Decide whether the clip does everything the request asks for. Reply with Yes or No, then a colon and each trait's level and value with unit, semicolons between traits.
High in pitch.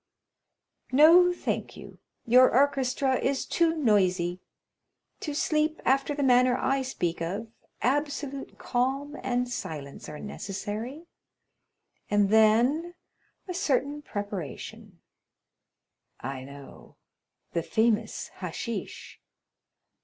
Yes: very high, 250 Hz